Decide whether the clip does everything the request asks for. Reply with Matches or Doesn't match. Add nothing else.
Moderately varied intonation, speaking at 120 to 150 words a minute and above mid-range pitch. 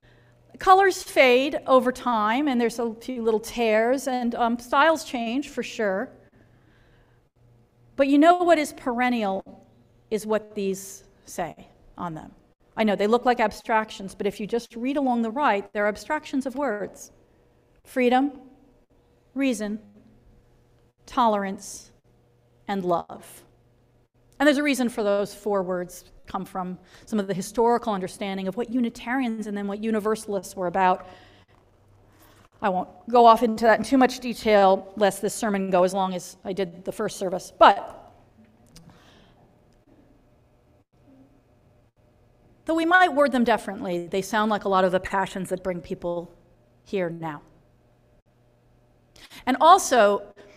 Doesn't match